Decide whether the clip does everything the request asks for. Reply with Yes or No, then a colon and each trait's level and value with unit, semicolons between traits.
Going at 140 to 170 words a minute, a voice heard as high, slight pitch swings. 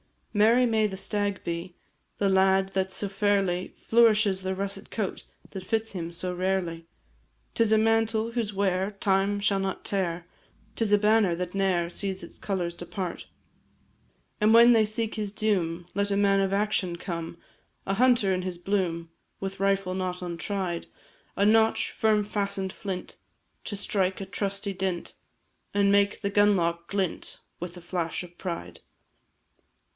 Yes: average, 160 wpm; high, 195 Hz; narrow, 2.3 semitones